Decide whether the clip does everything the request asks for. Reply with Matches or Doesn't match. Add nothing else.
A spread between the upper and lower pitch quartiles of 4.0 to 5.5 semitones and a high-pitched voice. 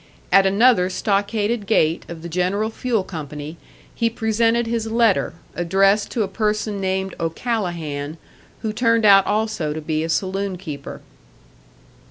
Matches